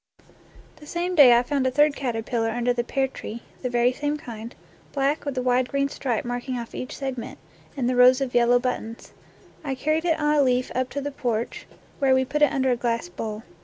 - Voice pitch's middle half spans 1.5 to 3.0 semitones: Yes, narrow, 2.6 semitones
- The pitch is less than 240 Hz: No, very high, 255 Hz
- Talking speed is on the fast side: Yes, fast, 220 wpm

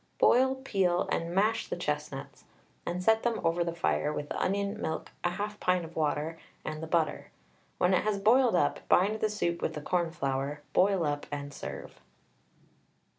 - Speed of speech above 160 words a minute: Yes, average, 175 wpm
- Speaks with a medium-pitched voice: Yes, medium, 175 Hz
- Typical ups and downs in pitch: Yes, average, 4.5 semitones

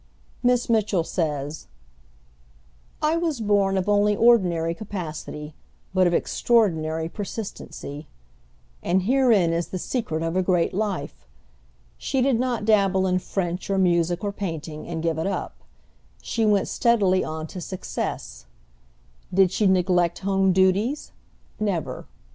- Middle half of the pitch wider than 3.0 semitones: Yes, average, 3.9 semitones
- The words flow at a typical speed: No, slow, 130 wpm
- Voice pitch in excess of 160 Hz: Yes, high, 190 Hz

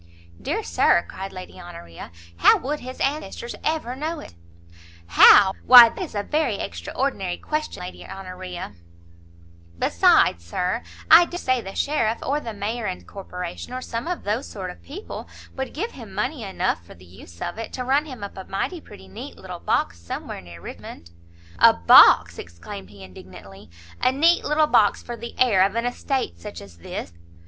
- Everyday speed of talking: Yes, average, 180 wpm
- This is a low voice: No, high, 205 Hz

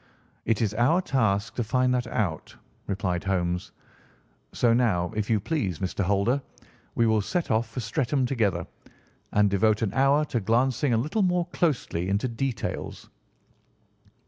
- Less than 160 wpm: Yes, average, 150 wpm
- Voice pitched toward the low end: Yes, low, 115 Hz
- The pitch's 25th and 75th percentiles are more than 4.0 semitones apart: Yes, average, 4.5 semitones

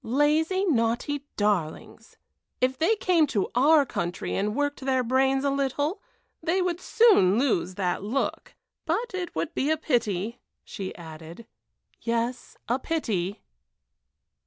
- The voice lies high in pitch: Yes, very high, 260 Hz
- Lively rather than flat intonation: Yes, wide, 7.0 semitones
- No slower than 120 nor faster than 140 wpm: Yes, slow, 135 wpm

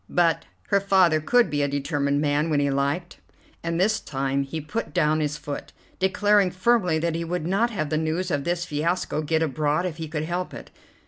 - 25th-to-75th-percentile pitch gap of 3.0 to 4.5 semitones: Yes, average, 3.6 semitones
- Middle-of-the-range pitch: Yes, medium, 160 Hz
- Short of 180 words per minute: No, fast, 205 wpm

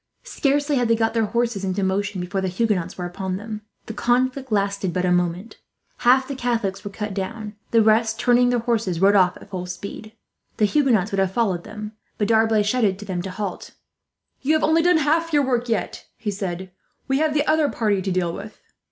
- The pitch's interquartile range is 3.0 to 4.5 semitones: Yes, average, 4.1 semitones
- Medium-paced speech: No, fast, 210 wpm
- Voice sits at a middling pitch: No, high, 215 Hz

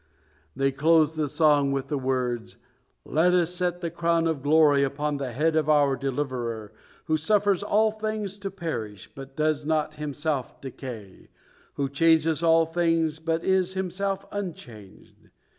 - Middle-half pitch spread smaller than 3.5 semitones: No, average, 3.8 semitones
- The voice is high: No, medium, 155 Hz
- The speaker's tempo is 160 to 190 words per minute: No, average, 150 wpm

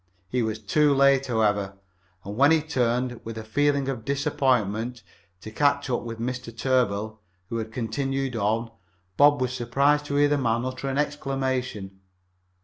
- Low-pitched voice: Yes, low, 125 Hz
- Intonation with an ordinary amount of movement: Yes, average, 3.6 semitones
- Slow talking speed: No, average, 160 wpm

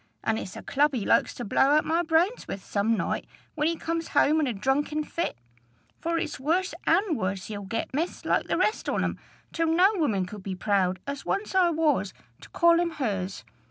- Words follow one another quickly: Yes, fast, 215 wpm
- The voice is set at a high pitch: Yes, very high, 295 Hz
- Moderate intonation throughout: No, wide, 8.1 semitones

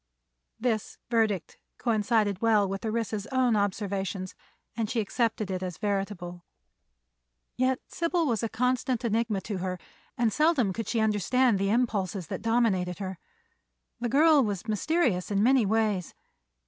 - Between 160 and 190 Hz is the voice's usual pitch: No, high, 215 Hz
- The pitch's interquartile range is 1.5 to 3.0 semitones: No, average, 3.5 semitones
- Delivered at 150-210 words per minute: No, average, 140 wpm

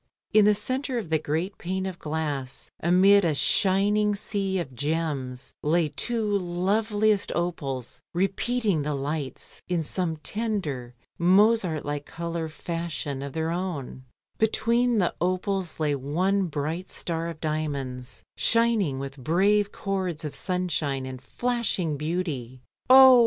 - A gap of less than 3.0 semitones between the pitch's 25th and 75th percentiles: No, average, 5.3 semitones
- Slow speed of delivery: Yes, slow, 130 wpm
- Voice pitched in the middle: Yes, medium, 170 Hz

